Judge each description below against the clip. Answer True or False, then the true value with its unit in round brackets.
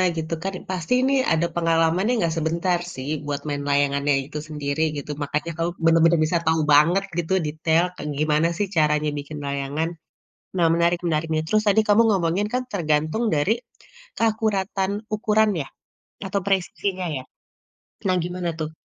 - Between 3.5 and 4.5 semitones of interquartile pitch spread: True (3.8 semitones)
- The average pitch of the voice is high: False (165 Hz)